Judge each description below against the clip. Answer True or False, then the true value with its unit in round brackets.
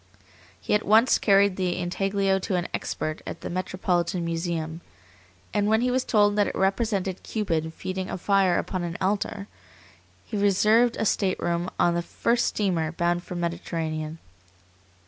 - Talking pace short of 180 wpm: True (160 wpm)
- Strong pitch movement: False (3.0 semitones)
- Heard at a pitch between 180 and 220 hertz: True (185 Hz)